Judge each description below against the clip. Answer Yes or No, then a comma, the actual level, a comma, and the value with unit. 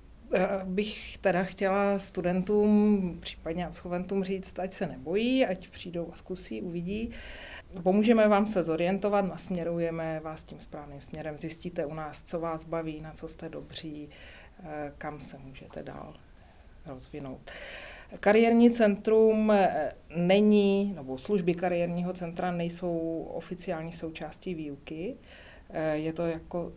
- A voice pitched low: No, medium, 180 Hz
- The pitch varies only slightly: No, average, 3.6 semitones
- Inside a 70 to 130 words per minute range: Yes, average, 120 wpm